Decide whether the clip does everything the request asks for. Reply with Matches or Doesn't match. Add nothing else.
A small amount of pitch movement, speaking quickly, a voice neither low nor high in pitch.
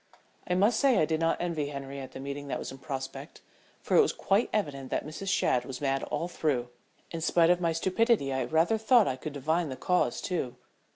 Doesn't match